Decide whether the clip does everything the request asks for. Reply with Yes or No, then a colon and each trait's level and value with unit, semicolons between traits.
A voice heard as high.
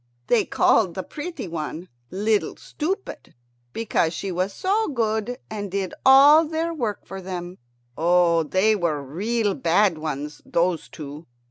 Yes: high, 195 Hz